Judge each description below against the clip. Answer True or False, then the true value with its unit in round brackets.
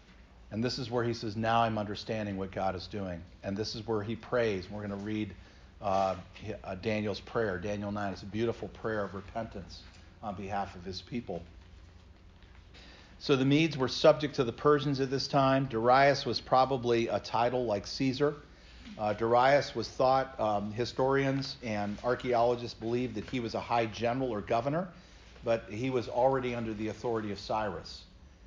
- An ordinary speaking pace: True (175 wpm)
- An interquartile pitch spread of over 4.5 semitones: False (4.0 semitones)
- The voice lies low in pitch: True (110 Hz)